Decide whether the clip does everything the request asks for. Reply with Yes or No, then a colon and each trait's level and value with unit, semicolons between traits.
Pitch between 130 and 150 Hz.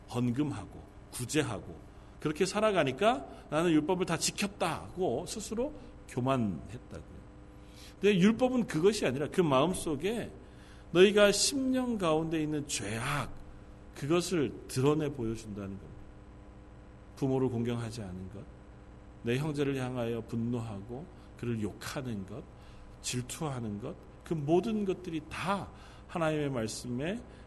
Yes: medium, 140 Hz